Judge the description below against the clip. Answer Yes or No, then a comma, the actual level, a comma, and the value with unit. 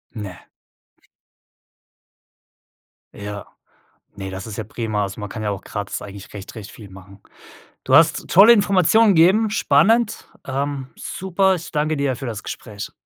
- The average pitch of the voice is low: Yes, low, 120 Hz